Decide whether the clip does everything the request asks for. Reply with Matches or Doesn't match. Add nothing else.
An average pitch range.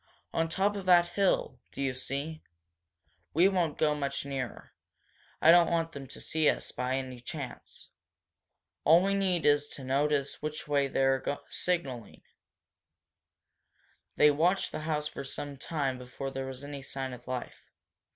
Matches